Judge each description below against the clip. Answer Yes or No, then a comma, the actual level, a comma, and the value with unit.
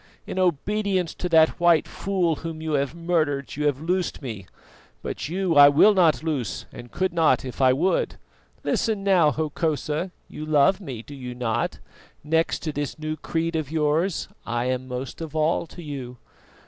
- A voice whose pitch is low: No, medium, 155 Hz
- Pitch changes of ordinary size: Yes, average, 3.8 semitones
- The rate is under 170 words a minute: No, average, 175 wpm